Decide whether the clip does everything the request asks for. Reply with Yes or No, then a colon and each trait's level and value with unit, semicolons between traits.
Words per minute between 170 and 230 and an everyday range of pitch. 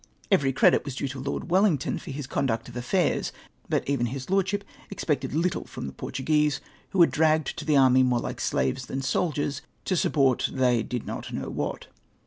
Yes: average, 190 wpm; average, 3.6 semitones